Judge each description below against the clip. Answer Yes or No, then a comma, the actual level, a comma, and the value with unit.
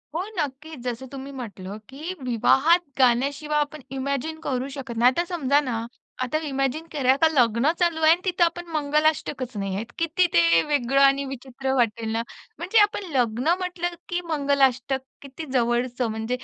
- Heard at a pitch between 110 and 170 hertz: No, very high, 275 Hz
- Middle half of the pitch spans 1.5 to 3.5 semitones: No, average, 4.1 semitones